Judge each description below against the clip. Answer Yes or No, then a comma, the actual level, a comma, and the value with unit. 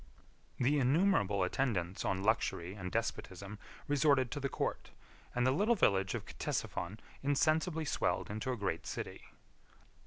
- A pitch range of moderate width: No, wide, 6.7 semitones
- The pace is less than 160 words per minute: Yes, average, 145 wpm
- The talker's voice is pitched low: Yes, low, 125 Hz